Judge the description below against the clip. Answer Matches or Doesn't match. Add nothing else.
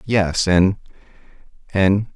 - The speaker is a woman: Doesn't match